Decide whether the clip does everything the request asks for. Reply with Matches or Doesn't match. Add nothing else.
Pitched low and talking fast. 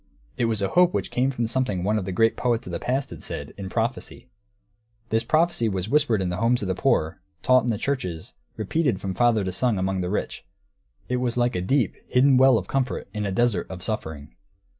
Matches